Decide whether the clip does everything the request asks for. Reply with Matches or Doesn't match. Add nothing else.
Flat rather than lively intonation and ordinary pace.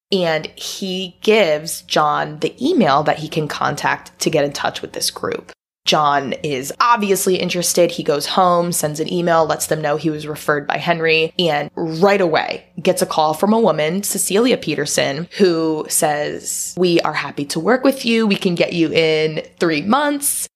Doesn't match